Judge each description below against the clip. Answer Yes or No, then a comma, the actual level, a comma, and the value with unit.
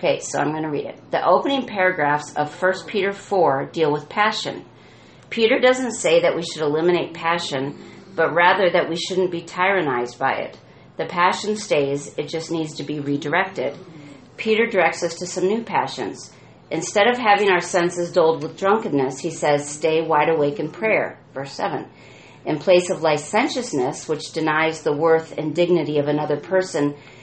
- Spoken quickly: No, average, 175 wpm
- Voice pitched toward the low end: No, medium, 170 Hz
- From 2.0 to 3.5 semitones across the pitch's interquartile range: No, average, 3.9 semitones